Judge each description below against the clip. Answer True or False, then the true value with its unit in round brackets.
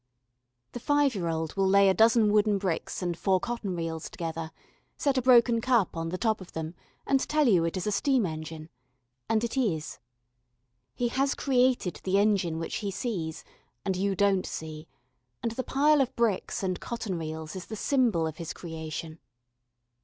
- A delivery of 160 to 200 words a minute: True (185 wpm)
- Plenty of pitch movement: True (6.2 semitones)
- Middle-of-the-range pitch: False (195 Hz)